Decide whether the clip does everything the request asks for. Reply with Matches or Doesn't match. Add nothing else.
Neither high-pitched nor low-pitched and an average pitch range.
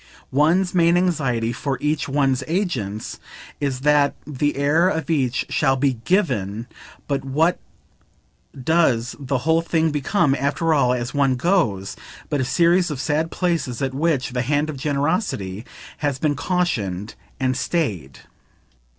Matches